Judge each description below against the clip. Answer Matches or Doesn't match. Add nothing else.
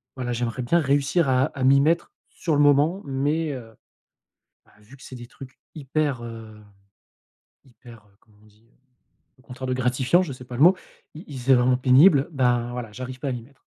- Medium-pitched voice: Doesn't match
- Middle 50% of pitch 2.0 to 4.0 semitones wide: Matches